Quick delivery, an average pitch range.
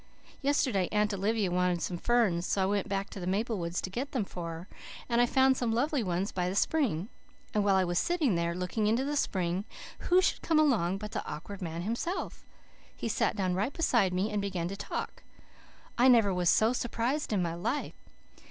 Yes: fast, 210 wpm; average, 4.9 semitones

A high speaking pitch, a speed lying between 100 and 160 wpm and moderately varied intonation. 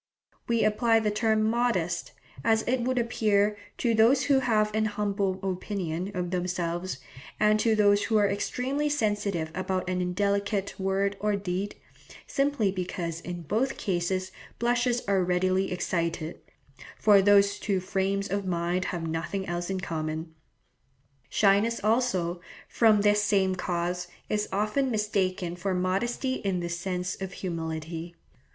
Yes: high, 195 Hz; average, 140 wpm; average, 3.1 semitones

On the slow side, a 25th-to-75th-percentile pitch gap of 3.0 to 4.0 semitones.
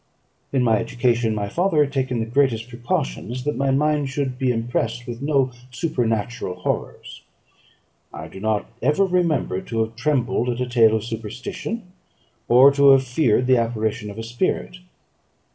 No: average, 160 wpm; average, 3.4 semitones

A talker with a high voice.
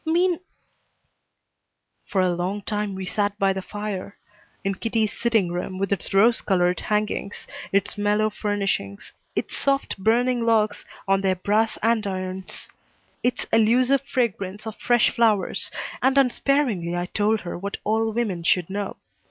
Yes: high, 205 Hz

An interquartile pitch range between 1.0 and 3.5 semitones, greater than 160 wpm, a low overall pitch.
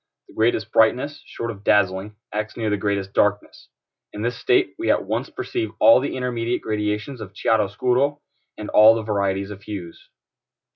Yes: average, 3.1 semitones; average, 175 wpm; low, 105 Hz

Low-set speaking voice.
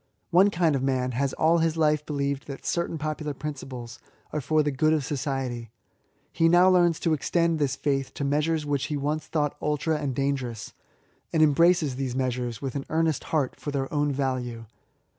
No: medium, 145 Hz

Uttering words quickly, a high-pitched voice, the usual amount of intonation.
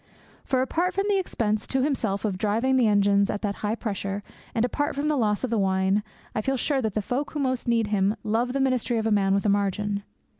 Yes: fast, 245 wpm; high, 220 Hz; average, 4.3 semitones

